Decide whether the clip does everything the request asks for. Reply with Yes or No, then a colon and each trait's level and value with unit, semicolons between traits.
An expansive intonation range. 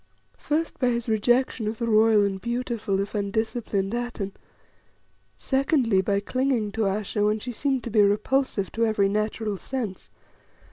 No: average, 3.0 semitones